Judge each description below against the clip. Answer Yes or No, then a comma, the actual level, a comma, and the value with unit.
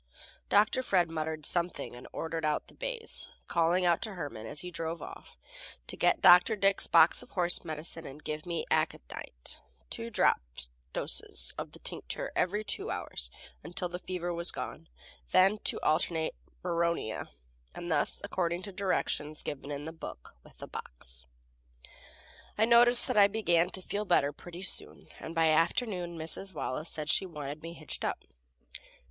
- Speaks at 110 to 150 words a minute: No, average, 165 wpm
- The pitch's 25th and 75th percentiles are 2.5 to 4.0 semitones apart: Yes, average, 3.2 semitones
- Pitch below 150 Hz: No, medium, 170 Hz